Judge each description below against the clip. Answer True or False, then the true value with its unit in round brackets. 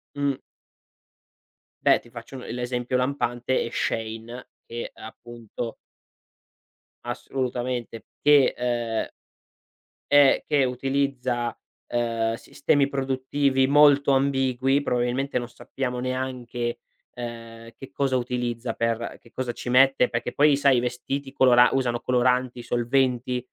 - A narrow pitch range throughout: True (2.0 semitones)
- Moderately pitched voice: False (125 Hz)